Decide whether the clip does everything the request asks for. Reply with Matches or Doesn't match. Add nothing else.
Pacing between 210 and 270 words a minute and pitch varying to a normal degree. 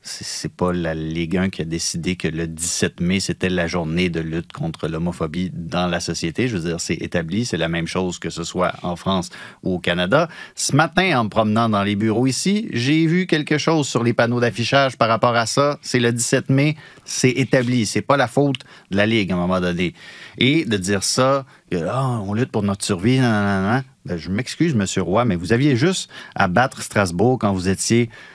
Doesn't match